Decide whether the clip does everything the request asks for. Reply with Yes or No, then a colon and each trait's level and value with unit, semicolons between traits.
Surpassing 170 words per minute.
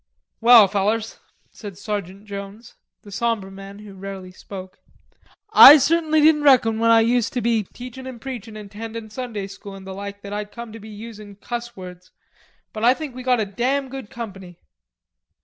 Yes: average, 185 wpm